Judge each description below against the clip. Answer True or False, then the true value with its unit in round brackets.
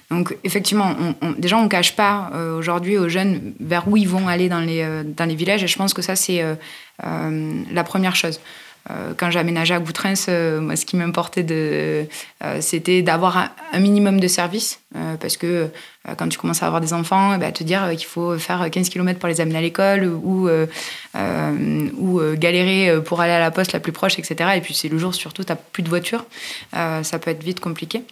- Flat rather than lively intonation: True (2.3 semitones)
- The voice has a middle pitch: True (175 Hz)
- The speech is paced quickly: True (230 wpm)